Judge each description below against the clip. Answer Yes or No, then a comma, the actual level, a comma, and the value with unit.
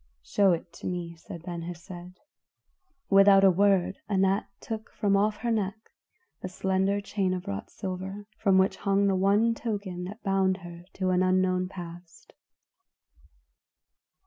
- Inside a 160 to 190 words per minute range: No, average, 145 wpm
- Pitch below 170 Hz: No, high, 190 Hz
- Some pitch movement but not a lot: No, narrow, 1.8 semitones